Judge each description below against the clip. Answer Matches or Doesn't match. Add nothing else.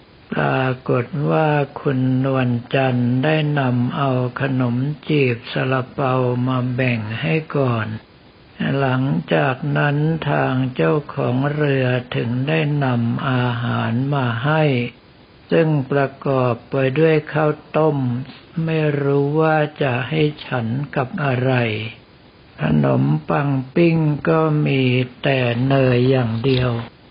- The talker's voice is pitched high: Doesn't match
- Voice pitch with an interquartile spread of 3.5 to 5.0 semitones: Doesn't match